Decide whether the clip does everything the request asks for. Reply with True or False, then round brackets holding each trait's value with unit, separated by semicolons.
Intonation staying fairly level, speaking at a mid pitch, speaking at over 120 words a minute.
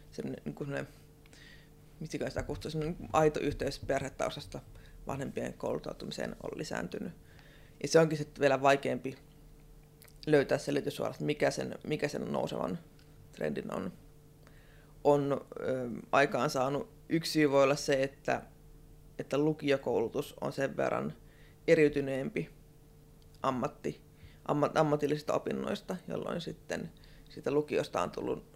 False (1.4 semitones; 150 Hz; 115 wpm)